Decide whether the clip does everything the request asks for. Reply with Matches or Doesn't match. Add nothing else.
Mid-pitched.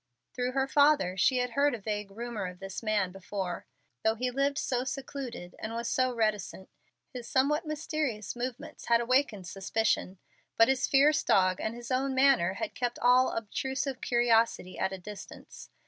Doesn't match